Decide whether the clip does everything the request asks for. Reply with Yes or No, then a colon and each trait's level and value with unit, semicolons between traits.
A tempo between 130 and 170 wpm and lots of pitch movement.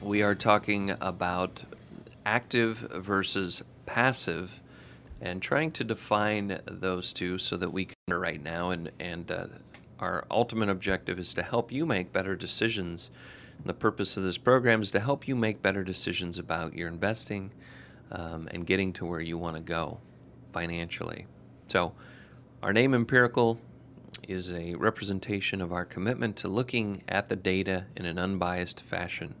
No: average, 155 wpm; average, 3.8 semitones